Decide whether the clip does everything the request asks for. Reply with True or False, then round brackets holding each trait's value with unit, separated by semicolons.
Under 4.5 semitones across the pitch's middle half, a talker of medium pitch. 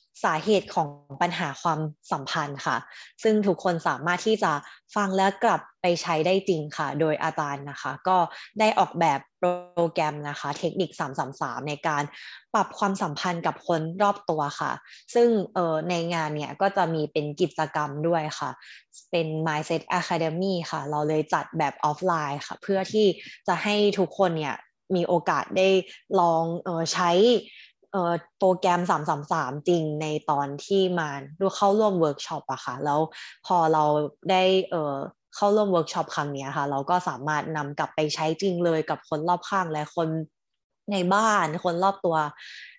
True (3.6 semitones; 170 Hz)